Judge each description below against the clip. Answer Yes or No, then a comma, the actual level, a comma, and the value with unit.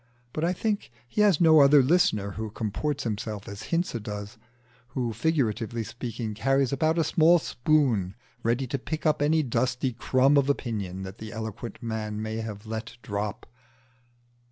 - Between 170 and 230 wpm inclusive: No, average, 160 wpm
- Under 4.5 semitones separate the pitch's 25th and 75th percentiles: No, average, 5.2 semitones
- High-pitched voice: No, low, 120 Hz